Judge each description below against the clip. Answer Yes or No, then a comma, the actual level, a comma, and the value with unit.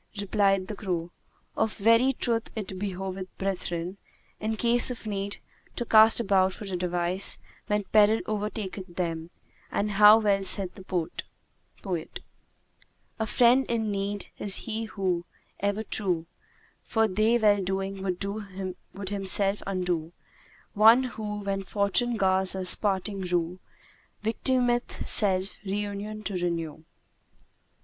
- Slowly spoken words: Yes, slow, 130 wpm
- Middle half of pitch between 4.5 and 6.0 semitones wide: No, narrow, 2.6 semitones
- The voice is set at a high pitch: Yes, high, 200 Hz